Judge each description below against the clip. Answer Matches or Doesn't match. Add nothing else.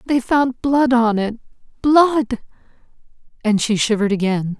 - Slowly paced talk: Matches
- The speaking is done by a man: Doesn't match